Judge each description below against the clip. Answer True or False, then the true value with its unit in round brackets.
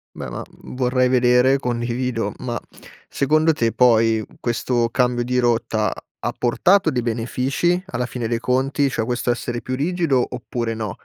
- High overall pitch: False (125 Hz)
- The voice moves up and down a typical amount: False (1.8 semitones)